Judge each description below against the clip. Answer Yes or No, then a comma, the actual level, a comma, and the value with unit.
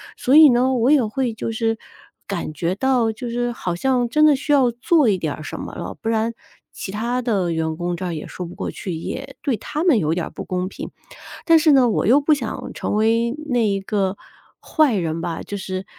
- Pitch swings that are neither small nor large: No, wide, 5.7 semitones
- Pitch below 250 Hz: Yes, high, 225 Hz